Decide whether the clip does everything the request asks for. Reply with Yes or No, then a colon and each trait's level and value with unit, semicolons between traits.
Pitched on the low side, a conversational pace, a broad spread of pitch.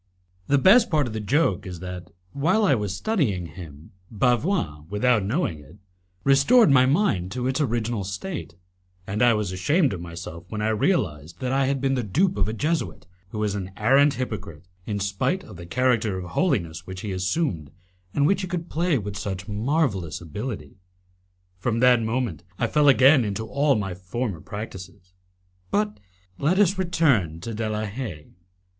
Yes: low, 110 Hz; average, 175 wpm; wide, 6.9 semitones